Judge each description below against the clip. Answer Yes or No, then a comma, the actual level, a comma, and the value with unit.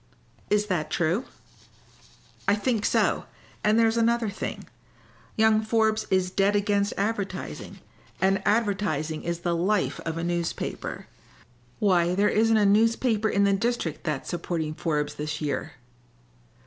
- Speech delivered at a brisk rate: No, slow, 135 wpm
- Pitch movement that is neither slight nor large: Yes, average, 4.2 semitones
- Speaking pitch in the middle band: No, high, 200 Hz